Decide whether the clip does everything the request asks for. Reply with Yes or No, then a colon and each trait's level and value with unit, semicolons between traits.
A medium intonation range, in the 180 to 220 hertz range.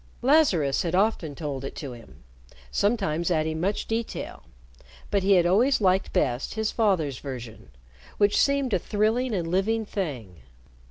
No: wide, 6.5 semitones; medium, 185 Hz